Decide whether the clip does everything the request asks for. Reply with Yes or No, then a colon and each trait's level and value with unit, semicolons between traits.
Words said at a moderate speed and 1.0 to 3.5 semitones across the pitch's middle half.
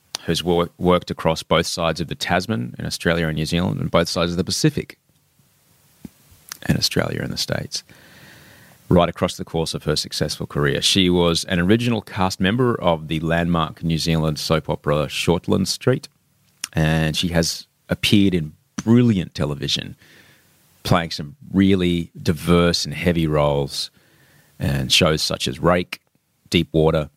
Yes: average, 150 wpm; narrow, 2.4 semitones